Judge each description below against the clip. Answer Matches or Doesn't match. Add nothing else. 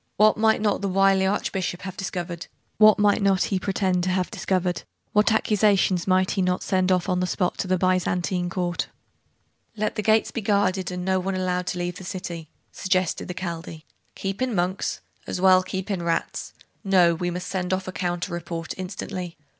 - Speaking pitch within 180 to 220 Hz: Matches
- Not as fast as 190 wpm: Doesn't match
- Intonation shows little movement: Matches